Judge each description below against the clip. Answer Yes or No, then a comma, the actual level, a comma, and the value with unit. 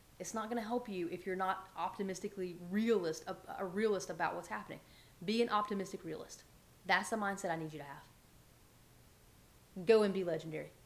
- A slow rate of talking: No, average, 175 wpm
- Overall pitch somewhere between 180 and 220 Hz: Yes, high, 190 Hz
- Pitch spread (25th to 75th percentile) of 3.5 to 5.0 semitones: No, average, 3.0 semitones